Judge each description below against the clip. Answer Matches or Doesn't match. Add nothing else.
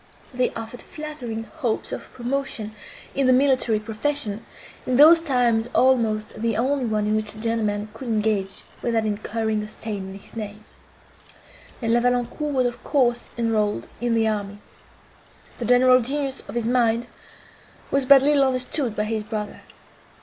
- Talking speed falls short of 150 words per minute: Doesn't match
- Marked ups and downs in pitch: Doesn't match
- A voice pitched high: Matches